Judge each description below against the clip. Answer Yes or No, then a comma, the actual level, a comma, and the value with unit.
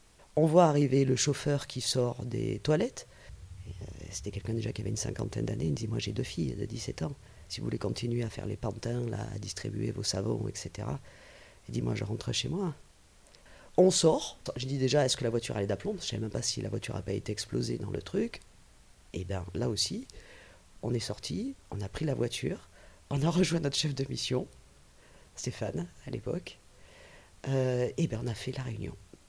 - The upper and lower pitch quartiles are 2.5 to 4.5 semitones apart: No, average, 5.2 semitones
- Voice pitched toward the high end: No, low, 115 Hz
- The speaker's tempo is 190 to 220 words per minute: Yes, average, 215 wpm